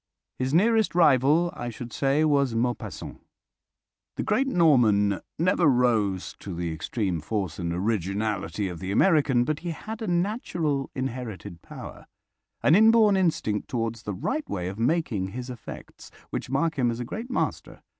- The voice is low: Yes, low, 125 Hz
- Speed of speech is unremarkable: Yes, average, 155 wpm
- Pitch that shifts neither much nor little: No, wide, 8.2 semitones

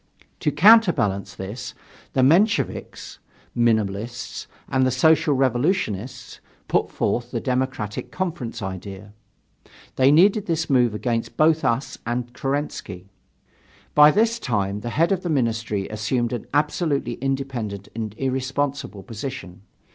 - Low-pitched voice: Yes, low, 125 Hz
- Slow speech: Yes, slow, 120 wpm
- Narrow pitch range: No, average, 5.2 semitones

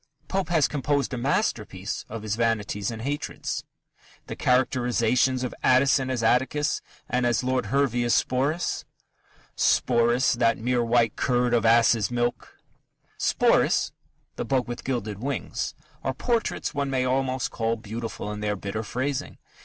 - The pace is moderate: Yes, average, 145 wpm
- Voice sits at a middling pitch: No, low, 125 Hz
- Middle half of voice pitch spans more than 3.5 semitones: No, narrow, 2.5 semitones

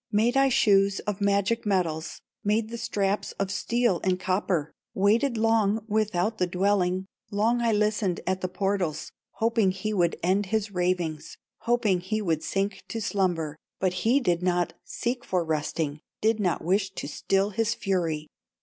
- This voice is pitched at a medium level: No, high, 195 Hz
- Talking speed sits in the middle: Yes, average, 160 wpm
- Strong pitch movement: No, average, 3.3 semitones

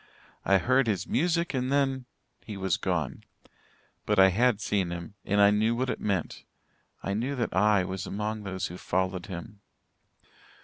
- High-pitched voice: No, low, 105 Hz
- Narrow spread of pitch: No, average, 4.5 semitones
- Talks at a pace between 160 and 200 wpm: Yes, average, 170 wpm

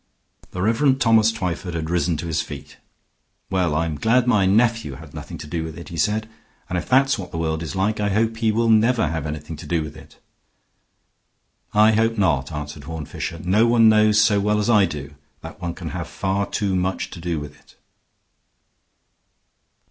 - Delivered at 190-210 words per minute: Yes, average, 200 wpm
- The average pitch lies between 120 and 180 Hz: No, very low, 95 Hz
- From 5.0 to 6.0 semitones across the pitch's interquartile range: Yes, wide, 5.4 semitones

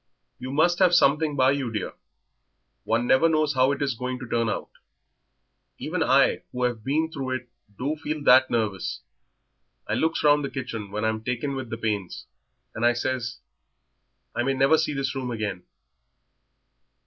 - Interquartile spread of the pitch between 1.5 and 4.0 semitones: Yes, average, 3.6 semitones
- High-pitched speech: No, low, 130 Hz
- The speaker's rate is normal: Yes, average, 170 wpm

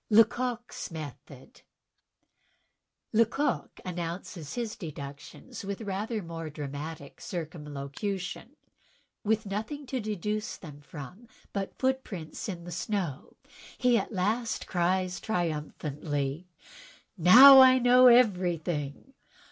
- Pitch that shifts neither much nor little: No, wide, 6.4 semitones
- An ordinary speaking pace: No, slow, 95 wpm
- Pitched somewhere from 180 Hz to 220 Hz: Yes, medium, 185 Hz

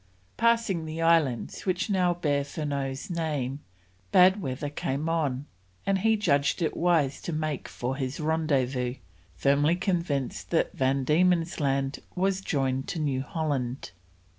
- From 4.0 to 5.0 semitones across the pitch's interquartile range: Yes, average, 4.3 semitones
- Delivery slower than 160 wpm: Yes, average, 140 wpm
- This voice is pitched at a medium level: Yes, medium, 150 Hz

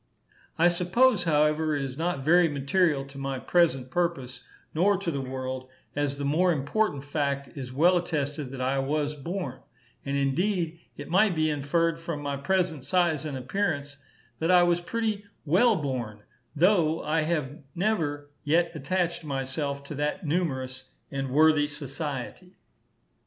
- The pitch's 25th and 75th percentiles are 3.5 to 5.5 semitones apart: Yes, average, 4.0 semitones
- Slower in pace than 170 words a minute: Yes, average, 150 wpm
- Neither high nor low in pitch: Yes, medium, 150 Hz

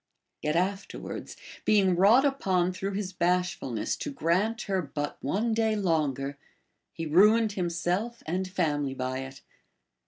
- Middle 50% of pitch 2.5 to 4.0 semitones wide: No, average, 5.1 semitones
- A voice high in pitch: No, medium, 180 Hz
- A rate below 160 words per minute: Yes, average, 145 wpm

